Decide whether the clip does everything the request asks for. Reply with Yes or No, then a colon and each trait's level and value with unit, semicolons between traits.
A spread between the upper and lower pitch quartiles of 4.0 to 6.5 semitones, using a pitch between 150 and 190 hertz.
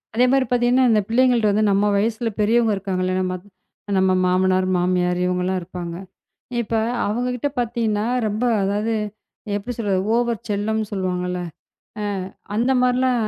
No: average, 4.3 semitones; high, 210 Hz